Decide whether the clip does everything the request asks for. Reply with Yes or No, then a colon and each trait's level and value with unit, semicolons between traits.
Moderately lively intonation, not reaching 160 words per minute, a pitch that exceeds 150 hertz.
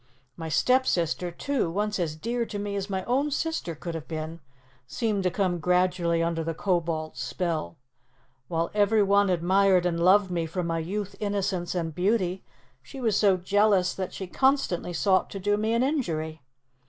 No: average, 3.5 semitones; average, 175 wpm; medium, 185 Hz